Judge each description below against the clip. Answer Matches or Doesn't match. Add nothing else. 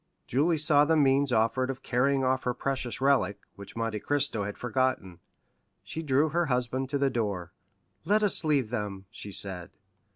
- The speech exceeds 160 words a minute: Matches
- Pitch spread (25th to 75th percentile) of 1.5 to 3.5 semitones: Doesn't match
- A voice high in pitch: Doesn't match